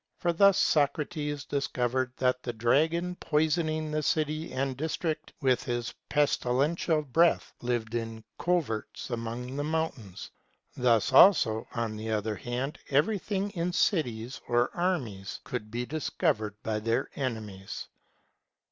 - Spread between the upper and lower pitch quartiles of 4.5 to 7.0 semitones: Yes, average, 5.2 semitones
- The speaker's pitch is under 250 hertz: Yes, low, 135 Hz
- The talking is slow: Yes, slow, 130 wpm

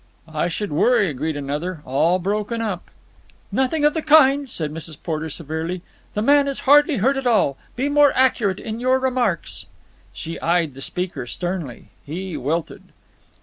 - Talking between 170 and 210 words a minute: No, average, 160 wpm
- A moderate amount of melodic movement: No, wide, 8.4 semitones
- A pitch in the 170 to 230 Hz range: Yes, medium, 185 Hz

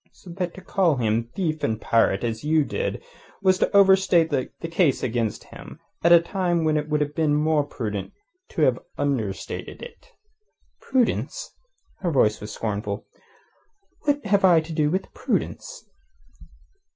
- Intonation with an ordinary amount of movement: No, wide, 7.4 semitones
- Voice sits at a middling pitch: Yes, medium, 155 Hz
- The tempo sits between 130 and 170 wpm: Yes, average, 155 wpm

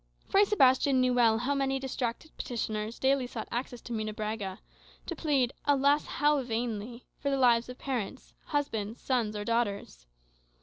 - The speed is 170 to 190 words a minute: No, average, 150 wpm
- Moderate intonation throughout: Yes, average, 3.6 semitones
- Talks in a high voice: Yes, high, 245 Hz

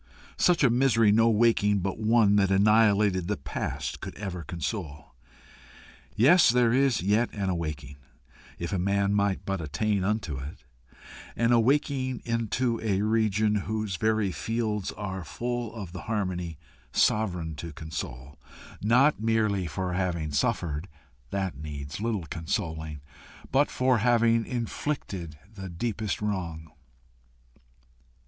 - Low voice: Yes, low, 100 Hz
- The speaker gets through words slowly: Yes, slow, 125 wpm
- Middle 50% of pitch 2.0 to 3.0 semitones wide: No, average, 4.8 semitones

